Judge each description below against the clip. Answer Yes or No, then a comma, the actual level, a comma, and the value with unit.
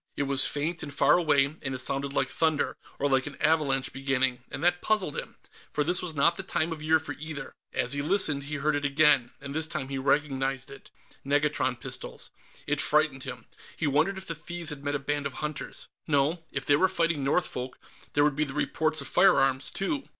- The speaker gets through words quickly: Yes, fast, 215 wpm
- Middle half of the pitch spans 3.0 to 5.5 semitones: No, narrow, 2.5 semitones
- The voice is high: No, medium, 145 Hz